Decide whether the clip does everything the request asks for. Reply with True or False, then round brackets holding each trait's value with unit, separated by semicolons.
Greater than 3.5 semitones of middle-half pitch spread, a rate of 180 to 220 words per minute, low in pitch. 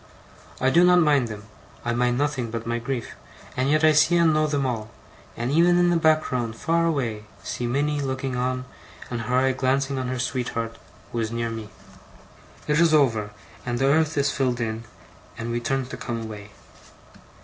True (4.1 semitones; 195 wpm; 130 Hz)